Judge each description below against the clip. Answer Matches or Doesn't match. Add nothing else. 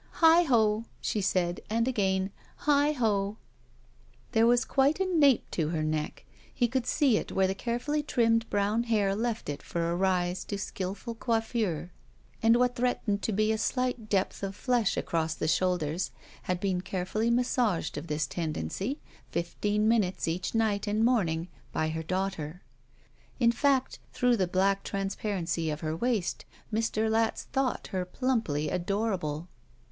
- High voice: Matches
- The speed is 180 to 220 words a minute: Doesn't match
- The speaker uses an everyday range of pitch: Matches